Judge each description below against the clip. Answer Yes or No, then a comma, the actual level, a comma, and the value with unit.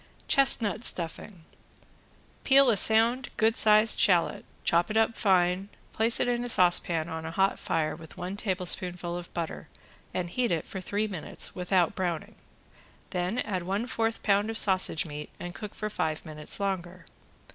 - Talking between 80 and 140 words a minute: No, average, 165 wpm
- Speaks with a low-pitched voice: No, medium, 185 Hz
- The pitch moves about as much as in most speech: Yes, average, 4.1 semitones